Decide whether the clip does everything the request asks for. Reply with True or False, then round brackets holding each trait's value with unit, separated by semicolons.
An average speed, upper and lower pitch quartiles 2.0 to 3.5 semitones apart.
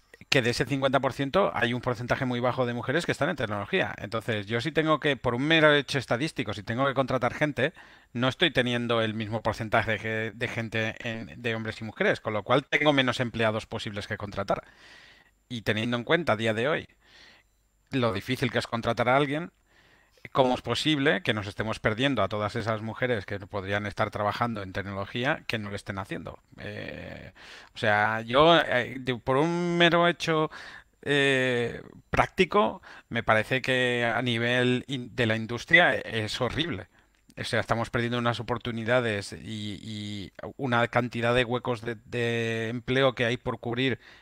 True (180 wpm; 2.9 semitones)